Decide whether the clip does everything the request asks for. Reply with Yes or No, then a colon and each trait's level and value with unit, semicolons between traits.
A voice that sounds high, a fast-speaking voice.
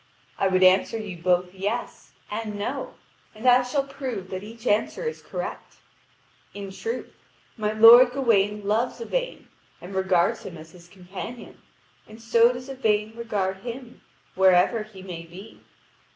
No: high, 210 Hz; average, 150 wpm